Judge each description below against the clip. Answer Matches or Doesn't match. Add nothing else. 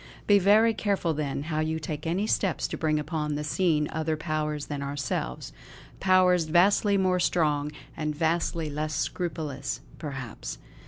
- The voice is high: Doesn't match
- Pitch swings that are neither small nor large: Matches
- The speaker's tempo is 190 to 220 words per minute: Doesn't match